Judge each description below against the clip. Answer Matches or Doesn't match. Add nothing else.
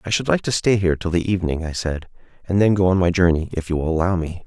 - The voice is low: Matches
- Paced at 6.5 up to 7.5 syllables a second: Matches